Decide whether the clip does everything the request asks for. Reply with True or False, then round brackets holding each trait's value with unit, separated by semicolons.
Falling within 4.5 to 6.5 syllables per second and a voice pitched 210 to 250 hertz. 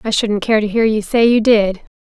True (5.1 syllables/s; 215 Hz)